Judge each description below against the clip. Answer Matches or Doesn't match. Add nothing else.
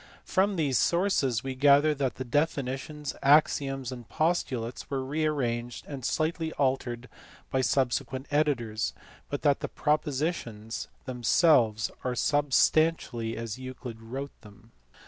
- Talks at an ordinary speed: Doesn't match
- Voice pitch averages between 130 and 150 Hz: Matches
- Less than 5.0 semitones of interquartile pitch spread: Matches